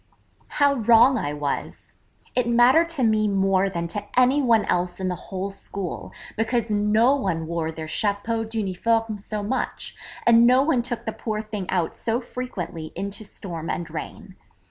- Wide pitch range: No, average, 4.2 semitones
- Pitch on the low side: No, high, 215 Hz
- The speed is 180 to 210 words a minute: No, average, 165 wpm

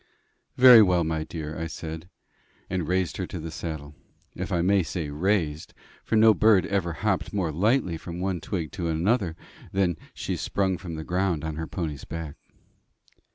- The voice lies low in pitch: Yes, very low, 85 Hz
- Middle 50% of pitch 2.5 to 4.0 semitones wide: Yes, average, 3.4 semitones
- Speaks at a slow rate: No, average, 175 wpm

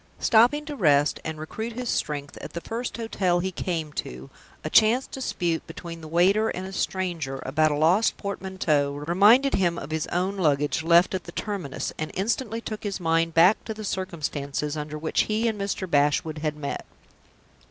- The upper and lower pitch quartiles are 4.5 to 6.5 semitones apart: Yes, average, 5.2 semitones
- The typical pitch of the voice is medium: Yes, medium, 175 Hz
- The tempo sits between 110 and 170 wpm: No, average, 185 wpm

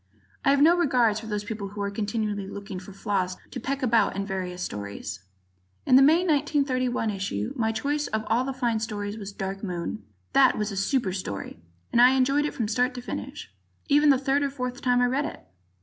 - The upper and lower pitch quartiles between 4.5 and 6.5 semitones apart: Yes, average, 5.0 semitones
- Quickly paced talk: Yes, fast, 210 wpm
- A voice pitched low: No, high, 225 Hz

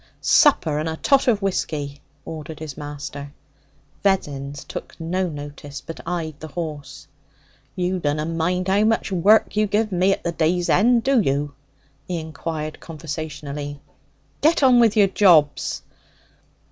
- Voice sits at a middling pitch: Yes, medium, 165 Hz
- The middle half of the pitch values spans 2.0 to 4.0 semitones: No, average, 4.8 semitones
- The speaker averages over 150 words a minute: No, average, 145 wpm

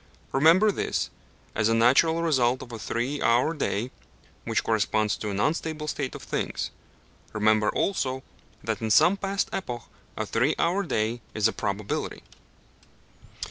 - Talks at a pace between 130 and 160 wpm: Yes, average, 145 wpm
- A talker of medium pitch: No, low, 125 Hz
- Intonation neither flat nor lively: No, wide, 6.5 semitones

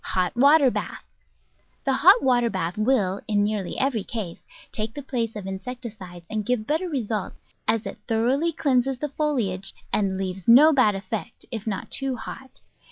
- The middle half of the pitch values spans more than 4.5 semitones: Yes, average, 5.1 semitones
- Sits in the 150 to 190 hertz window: No, high, 225 Hz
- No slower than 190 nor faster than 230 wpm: No, average, 165 wpm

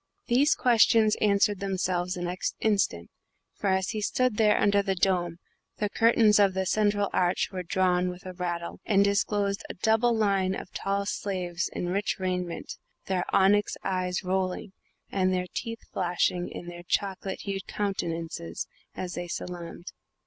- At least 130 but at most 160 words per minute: Yes, average, 155 wpm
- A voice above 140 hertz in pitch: Yes, high, 190 Hz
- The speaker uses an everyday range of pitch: No, narrow, 2.3 semitones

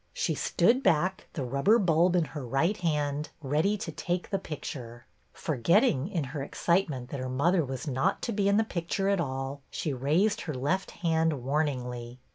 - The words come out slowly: No, average, 185 wpm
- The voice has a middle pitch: Yes, medium, 155 Hz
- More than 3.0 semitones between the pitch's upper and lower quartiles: Yes, wide, 5.4 semitones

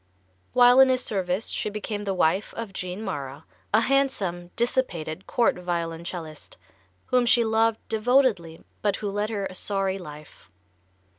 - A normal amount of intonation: Yes, average, 4.5 semitones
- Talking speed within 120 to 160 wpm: Yes, average, 145 wpm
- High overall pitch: Yes, high, 200 Hz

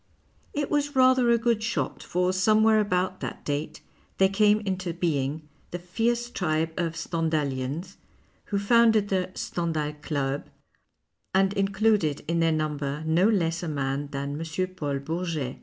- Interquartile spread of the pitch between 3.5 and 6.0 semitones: Yes, average, 5.2 semitones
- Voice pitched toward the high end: No, medium, 175 Hz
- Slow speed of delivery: No, average, 150 wpm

